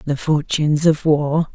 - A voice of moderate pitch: Yes, medium, 150 Hz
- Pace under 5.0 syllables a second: Yes, 4.4 syllables/s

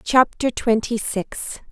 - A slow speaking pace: Yes, slow, 105 wpm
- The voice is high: Yes, high, 230 Hz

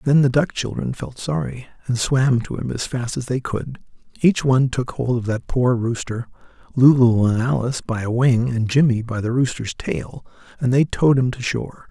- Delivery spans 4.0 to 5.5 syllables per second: Yes, 5.1 syllables/s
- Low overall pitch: Yes, low, 125 Hz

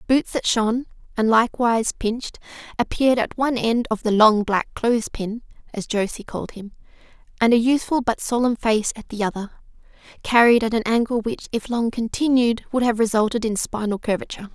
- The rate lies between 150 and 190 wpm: Yes, average, 170 wpm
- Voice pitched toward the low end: No, high, 230 Hz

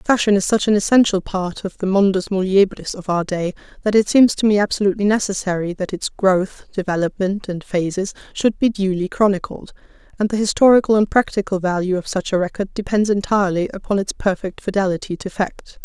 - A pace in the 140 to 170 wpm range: No, average, 180 wpm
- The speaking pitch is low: No, high, 195 Hz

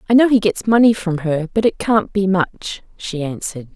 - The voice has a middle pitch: No, high, 195 Hz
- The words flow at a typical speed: No, fast, 225 wpm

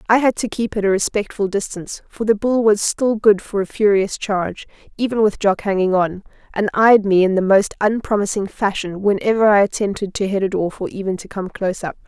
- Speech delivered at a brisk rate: Yes, fast, 220 wpm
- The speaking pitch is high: Yes, high, 205 Hz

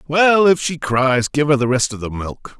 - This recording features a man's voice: Yes, male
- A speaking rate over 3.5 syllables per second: Yes, 4.6 syllables/s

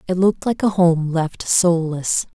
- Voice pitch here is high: No, medium, 175 Hz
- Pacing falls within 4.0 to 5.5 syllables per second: Yes, 4.2 syllables/s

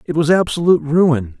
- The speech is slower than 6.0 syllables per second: Yes, 5.5 syllables/s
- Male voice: Yes, male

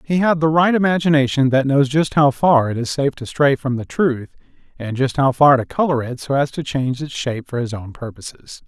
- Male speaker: Yes, male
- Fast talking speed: Yes, fast, 240 wpm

